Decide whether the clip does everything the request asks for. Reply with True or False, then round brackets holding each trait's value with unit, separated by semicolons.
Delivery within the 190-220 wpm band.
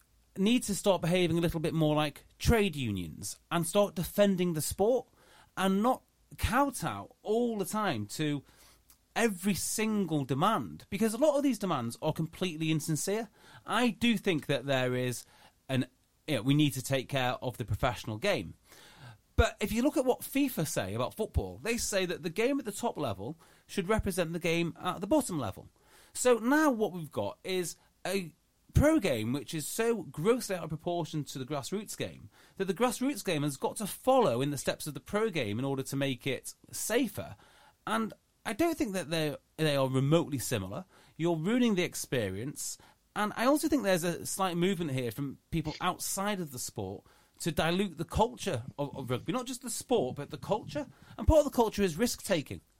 True (195 wpm)